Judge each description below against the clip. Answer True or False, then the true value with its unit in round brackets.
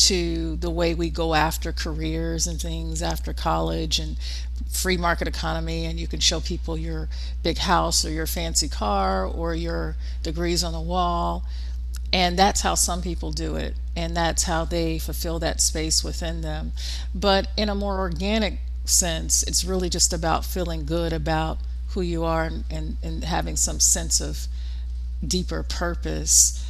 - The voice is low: True (80 Hz)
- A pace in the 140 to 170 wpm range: True (165 wpm)